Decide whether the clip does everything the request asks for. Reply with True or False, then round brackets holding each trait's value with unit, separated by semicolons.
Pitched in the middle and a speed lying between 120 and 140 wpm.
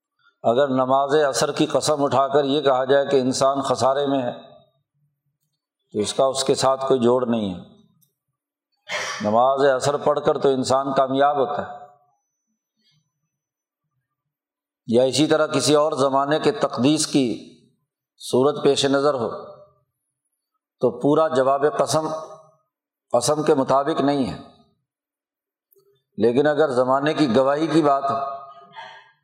True (145 Hz; 130 wpm)